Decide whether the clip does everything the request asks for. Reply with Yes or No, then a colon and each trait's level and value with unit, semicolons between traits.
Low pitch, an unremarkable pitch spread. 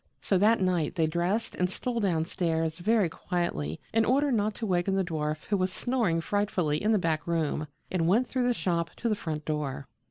No: medium, 180 Hz; average, 4.7 semitones